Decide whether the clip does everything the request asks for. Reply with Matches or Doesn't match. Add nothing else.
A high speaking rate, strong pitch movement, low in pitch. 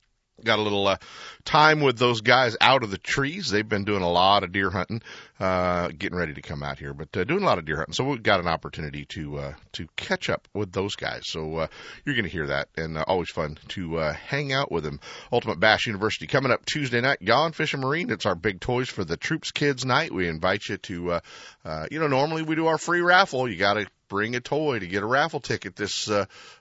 Matches